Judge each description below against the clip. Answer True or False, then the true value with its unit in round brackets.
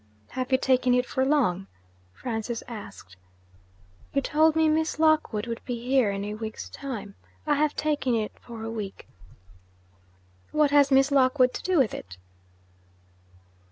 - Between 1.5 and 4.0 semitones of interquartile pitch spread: False (4.6 semitones)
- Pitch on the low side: False (255 Hz)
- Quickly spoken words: False (155 wpm)